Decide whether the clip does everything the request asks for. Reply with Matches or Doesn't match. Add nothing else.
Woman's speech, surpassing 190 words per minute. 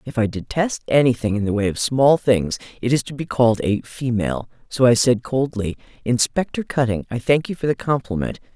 Matches